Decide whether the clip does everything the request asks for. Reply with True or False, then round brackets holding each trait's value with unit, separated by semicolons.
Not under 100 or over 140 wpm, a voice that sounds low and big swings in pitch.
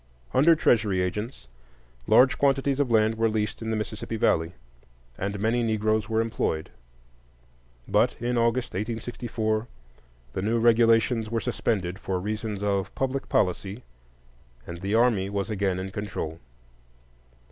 False (135 wpm; 110 Hz; 2.8 semitones)